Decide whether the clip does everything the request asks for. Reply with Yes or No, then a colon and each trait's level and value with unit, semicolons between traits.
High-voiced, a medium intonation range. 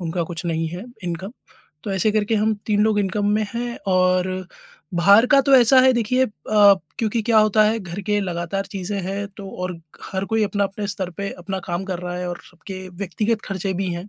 Yes: high, 195 Hz; average, 3.0 semitones